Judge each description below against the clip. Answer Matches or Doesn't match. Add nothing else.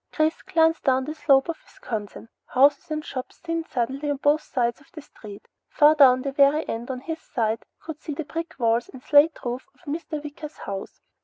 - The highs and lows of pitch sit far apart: Doesn't match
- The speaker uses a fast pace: Matches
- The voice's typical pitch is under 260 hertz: Doesn't match